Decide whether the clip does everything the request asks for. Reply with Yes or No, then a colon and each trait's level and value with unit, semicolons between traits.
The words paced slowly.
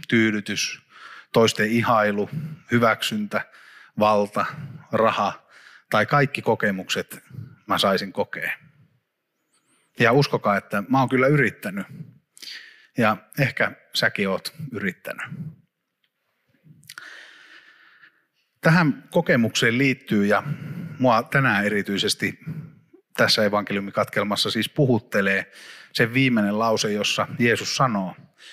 Yes: slow, 85 wpm